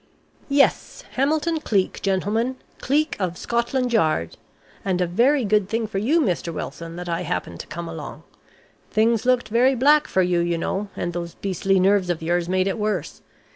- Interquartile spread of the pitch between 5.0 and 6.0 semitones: Yes, wide, 5.6 semitones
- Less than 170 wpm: No, average, 175 wpm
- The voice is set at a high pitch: Yes, high, 195 Hz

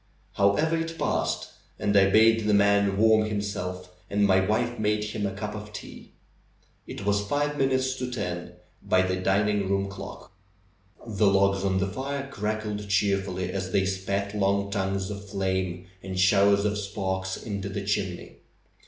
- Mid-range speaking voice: No, low, 100 Hz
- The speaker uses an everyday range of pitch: No, narrow, 1.6 semitones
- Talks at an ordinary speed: Yes, average, 165 wpm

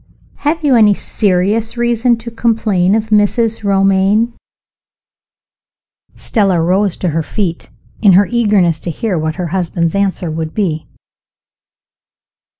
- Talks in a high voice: Yes, high, 200 Hz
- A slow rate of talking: Yes, slow, 125 wpm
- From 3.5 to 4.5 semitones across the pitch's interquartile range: Yes, average, 4.1 semitones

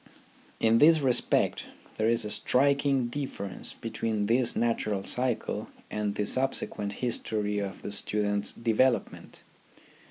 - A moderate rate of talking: No, slow, 120 wpm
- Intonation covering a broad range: No, average, 3.8 semitones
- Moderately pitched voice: No, low, 115 Hz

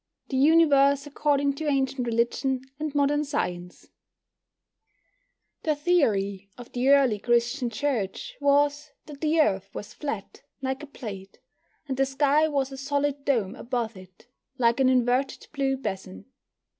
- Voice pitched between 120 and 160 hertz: No, very high, 270 Hz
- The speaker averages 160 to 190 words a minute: No, average, 140 wpm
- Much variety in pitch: No, average, 3.6 semitones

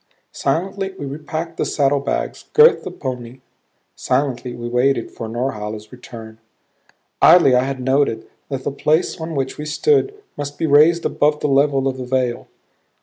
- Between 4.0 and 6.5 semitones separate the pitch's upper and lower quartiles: No, average, 3.3 semitones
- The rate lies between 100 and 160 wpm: Yes, average, 155 wpm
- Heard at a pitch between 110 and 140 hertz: Yes, low, 135 Hz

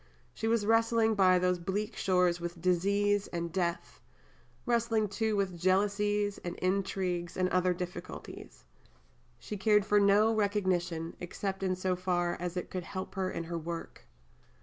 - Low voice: No, medium, 185 Hz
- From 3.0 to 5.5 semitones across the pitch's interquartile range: No, narrow, 2.6 semitones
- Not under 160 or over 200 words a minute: No, average, 150 wpm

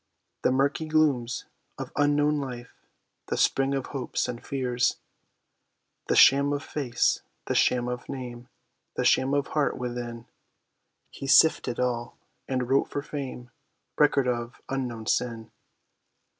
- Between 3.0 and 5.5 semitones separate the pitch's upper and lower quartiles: No, narrow, 2.5 semitones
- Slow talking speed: Yes, slow, 130 wpm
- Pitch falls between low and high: No, low, 130 Hz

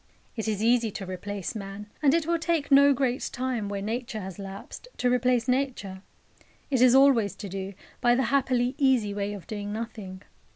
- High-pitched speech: Yes, high, 230 Hz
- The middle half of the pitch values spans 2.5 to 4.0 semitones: No, average, 4.4 semitones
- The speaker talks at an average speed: Yes, average, 190 wpm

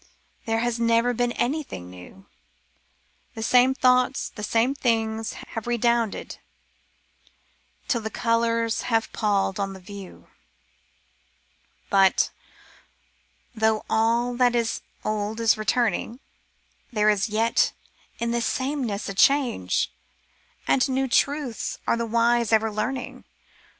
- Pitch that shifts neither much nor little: No, narrow, 2.1 semitones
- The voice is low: No, high, 230 Hz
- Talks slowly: Yes, slow, 120 wpm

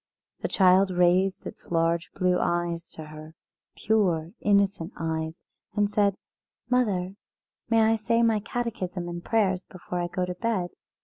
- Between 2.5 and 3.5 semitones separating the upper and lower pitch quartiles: Yes, average, 3.2 semitones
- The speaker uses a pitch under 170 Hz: No, medium, 185 Hz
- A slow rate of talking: No, average, 145 wpm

